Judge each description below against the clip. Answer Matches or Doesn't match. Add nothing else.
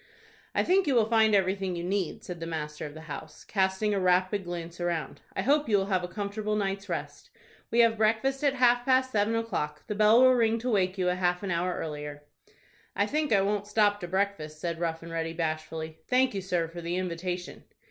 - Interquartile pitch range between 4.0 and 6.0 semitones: Matches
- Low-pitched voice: Doesn't match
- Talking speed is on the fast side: Matches